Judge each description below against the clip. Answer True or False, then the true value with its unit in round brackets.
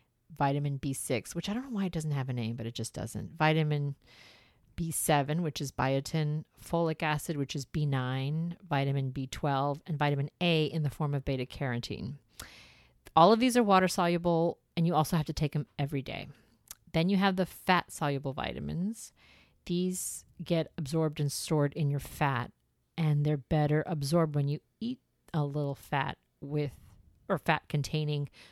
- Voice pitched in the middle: True (150 Hz)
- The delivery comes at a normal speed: True (170 wpm)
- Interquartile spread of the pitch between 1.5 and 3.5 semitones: True (3.1 semitones)